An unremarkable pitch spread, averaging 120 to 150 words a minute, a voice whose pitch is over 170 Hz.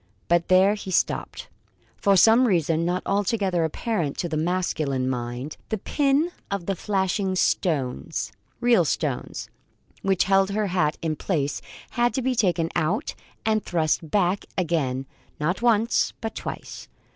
Yes: average, 4.7 semitones; average, 140 wpm; medium, 185 Hz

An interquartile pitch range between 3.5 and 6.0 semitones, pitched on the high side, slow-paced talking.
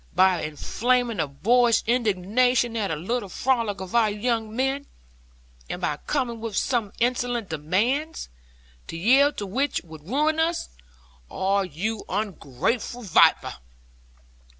Yes: average, 4.8 semitones; high, 225 Hz; slow, 125 wpm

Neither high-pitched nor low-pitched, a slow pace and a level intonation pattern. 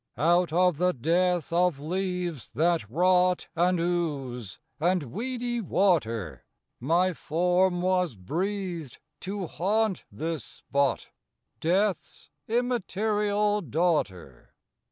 No: medium, 175 Hz; slow, 95 wpm; average, 3.3 semitones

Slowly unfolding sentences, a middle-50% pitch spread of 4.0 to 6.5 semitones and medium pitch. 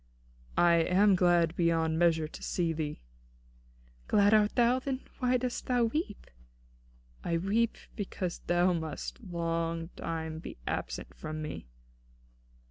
Yes: slow, 125 wpm; average, 4.4 semitones; medium, 175 Hz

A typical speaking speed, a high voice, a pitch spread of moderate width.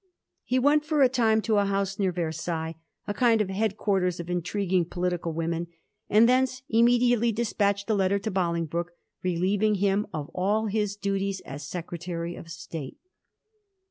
Yes: average, 160 wpm; high, 195 Hz; average, 4.0 semitones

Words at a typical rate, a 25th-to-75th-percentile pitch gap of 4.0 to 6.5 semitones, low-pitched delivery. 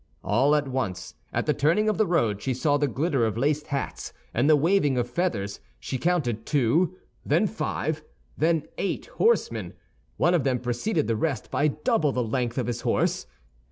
No: average, 185 wpm; average, 5.2 semitones; medium, 145 Hz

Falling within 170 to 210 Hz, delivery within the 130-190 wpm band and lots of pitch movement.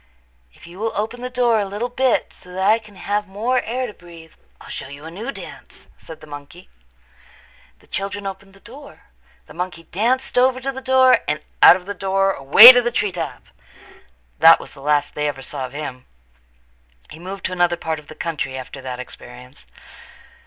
No: high, 190 Hz; average, 200 wpm; wide, 7.0 semitones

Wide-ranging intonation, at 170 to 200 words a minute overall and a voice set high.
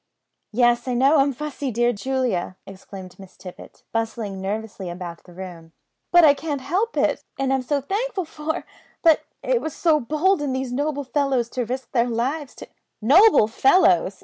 Yes: wide, 5.9 semitones; average, 175 wpm; very high, 260 Hz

